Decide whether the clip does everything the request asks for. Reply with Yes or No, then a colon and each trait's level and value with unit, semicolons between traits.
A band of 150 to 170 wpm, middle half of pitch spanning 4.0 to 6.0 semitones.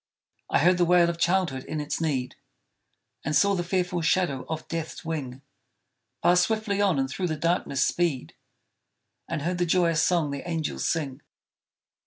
No: average, 165 wpm; average, 3.2 semitones